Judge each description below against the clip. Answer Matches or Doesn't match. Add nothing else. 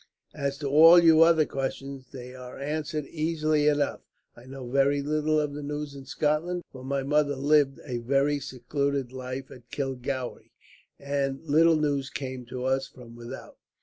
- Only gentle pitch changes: Matches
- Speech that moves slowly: Doesn't match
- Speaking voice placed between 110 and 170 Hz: Matches